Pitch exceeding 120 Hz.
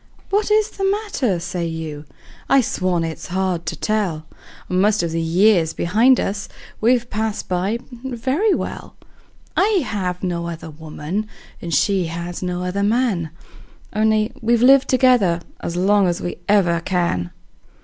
Yes: high, 190 Hz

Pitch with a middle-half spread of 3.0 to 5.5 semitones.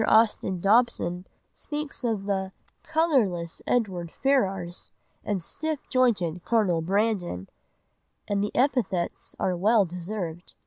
Yes: average, 5.0 semitones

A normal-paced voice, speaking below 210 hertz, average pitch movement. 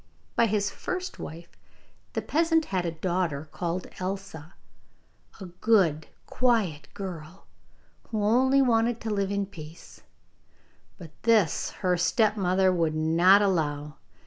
No: slow, 120 wpm; high, 190 Hz; average, 4.7 semitones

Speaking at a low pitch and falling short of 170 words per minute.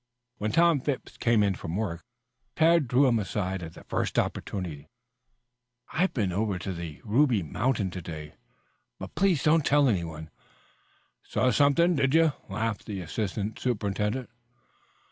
Yes: low, 110 Hz; average, 145 wpm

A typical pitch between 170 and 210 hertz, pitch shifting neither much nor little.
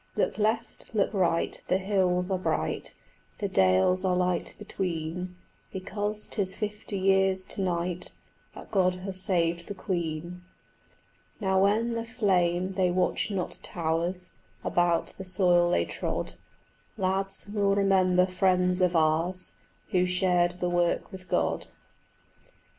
No: medium, 185 Hz; narrow, 1.6 semitones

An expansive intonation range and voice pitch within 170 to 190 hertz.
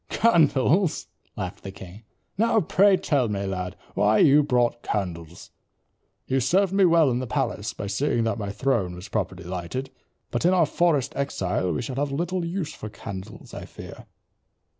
No: wide, 8.7 semitones; low, 130 Hz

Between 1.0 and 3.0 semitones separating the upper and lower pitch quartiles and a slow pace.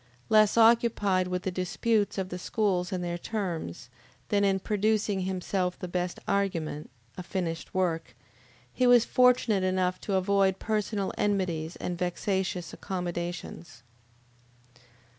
Yes: narrow, 2.5 semitones; slow, 125 wpm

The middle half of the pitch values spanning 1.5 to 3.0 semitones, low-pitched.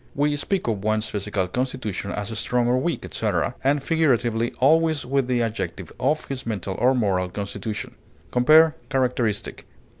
No: average, 4.6 semitones; low, 125 Hz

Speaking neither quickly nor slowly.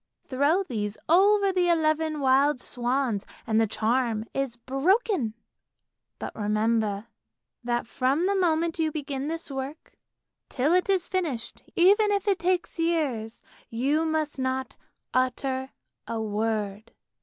No: slow, 130 wpm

